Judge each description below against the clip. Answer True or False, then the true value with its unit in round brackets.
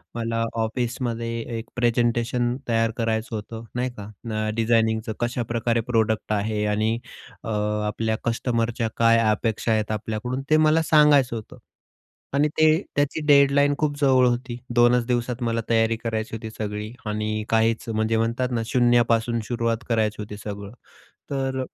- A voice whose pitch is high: False (115 Hz)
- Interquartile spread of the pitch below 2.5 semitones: True (1.8 semitones)